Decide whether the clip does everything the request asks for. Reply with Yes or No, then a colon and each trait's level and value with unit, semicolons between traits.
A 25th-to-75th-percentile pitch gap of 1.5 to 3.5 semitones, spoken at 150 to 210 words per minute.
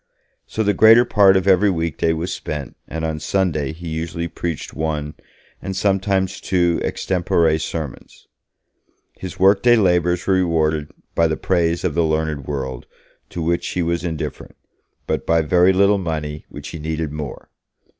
Yes: average, 3.1 semitones; average, 155 wpm